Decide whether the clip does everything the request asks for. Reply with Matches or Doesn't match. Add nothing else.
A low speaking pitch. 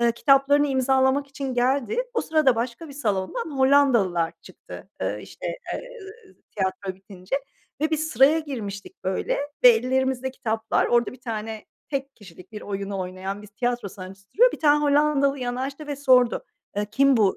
Doesn't match